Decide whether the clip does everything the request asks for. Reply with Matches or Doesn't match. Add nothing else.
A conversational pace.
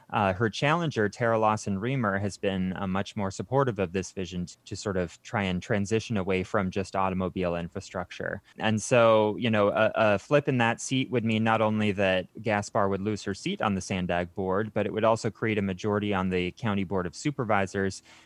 Doesn't match